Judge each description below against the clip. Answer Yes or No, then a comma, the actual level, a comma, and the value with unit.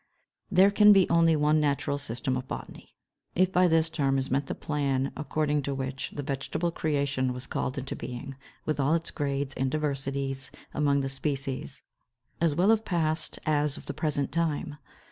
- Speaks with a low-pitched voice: No, medium, 145 Hz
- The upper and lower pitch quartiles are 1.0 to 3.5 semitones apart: Yes, narrow, 2.6 semitones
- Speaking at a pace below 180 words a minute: No, average, 185 wpm